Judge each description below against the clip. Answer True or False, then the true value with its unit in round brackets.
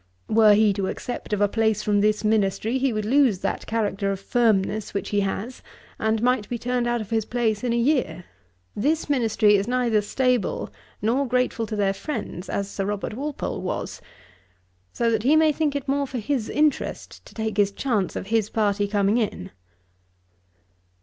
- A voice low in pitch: False (220 Hz)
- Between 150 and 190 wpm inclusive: True (185 wpm)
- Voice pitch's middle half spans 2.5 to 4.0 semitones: True (3.4 semitones)